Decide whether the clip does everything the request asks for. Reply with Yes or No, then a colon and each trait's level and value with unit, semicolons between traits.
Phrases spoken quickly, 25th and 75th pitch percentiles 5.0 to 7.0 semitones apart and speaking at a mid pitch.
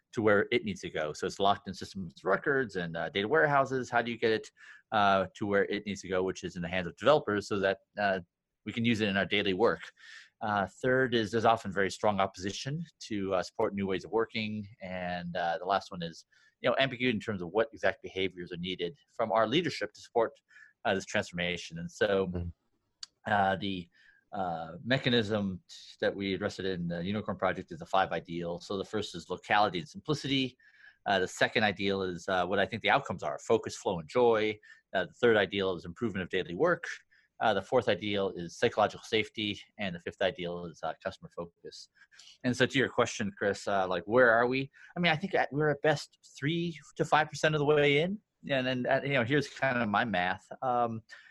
No: fast, 220 wpm; wide, 5.5 semitones; low, 105 Hz